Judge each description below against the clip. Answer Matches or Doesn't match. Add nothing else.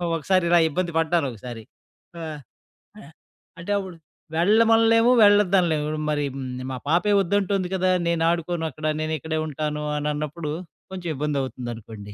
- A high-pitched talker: Doesn't match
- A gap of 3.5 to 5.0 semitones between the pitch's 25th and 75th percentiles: Matches